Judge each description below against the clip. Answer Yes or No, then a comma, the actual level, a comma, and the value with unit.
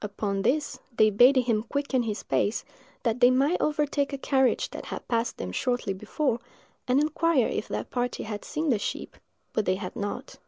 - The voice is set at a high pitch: Yes, high, 245 Hz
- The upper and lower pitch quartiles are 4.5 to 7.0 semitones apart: Yes, average, 4.8 semitones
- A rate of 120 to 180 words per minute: No, average, 190 wpm